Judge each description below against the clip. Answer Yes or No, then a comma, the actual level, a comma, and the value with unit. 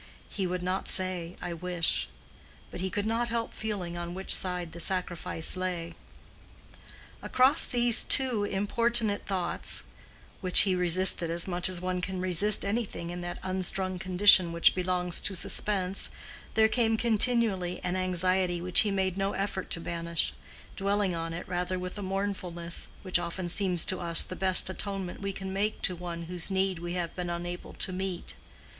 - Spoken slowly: No, average, 165 wpm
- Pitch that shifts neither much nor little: No, narrow, 2.0 semitones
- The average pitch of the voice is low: No, medium, 185 Hz